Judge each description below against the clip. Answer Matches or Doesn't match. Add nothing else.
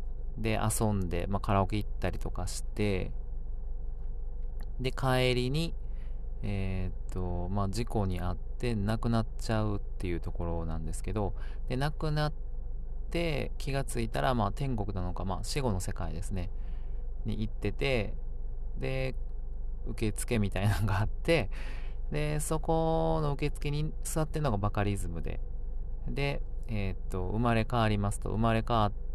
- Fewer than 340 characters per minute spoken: Matches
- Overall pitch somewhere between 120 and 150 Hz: Doesn't match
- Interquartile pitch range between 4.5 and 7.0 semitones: Matches